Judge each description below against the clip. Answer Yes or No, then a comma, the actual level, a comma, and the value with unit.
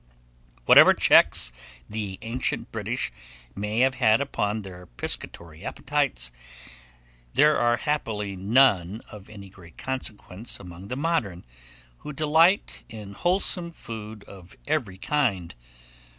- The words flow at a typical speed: No, slow, 115 wpm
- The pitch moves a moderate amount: No, wide, 5.7 semitones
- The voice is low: Yes, low, 110 Hz